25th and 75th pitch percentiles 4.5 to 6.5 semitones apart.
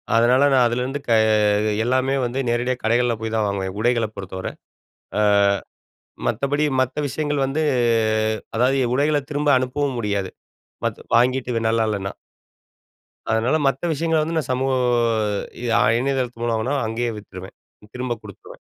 No: average, 3.2 semitones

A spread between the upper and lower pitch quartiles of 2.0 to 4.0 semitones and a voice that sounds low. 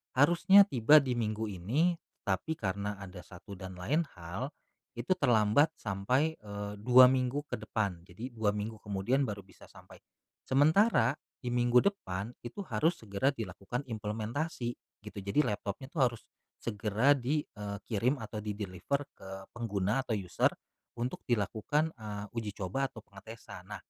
No: average, 4.7 semitones; low, 110 Hz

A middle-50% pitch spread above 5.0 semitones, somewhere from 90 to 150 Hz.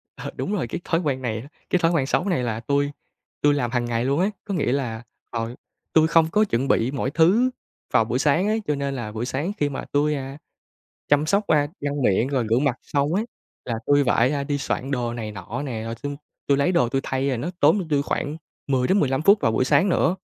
No: average, 4.2 semitones; medium, 140 Hz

